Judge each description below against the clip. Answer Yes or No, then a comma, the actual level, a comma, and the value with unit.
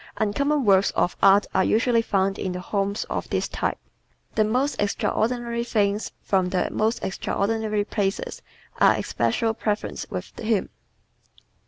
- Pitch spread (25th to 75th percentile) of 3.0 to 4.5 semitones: No, narrow, 2.6 semitones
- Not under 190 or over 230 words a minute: No, average, 140 wpm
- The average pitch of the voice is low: No, high, 210 Hz